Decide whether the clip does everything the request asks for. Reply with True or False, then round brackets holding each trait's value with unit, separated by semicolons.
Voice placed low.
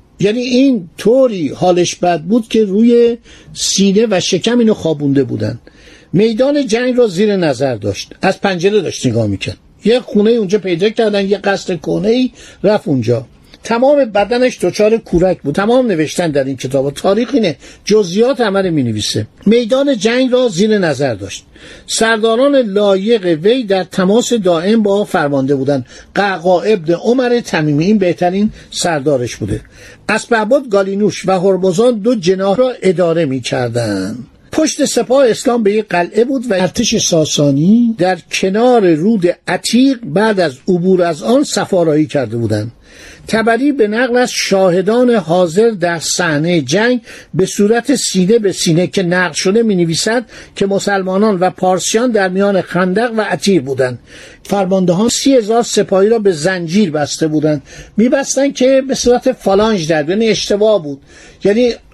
False (200 Hz)